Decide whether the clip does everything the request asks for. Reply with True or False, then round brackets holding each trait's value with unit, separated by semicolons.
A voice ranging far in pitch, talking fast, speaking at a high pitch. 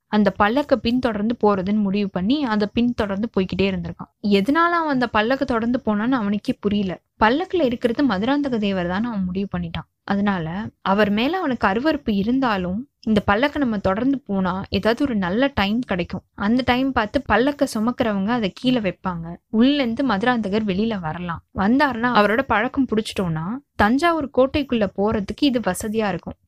False (4.3 semitones; 145 wpm; 220 Hz)